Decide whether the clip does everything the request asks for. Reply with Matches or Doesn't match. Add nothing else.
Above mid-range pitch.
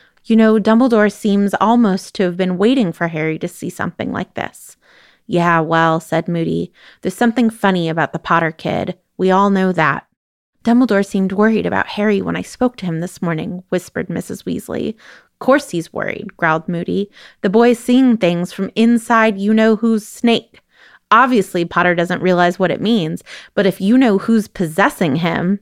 Matches